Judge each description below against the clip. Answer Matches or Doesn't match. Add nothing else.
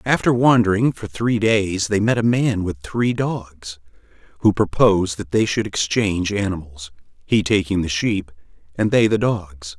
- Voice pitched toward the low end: Matches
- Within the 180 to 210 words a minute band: Doesn't match